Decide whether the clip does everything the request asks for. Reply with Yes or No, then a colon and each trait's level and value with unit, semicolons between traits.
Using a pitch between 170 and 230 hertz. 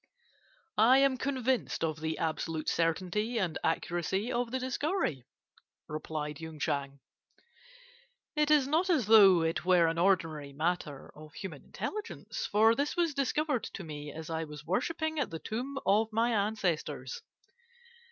Yes: high, 190 Hz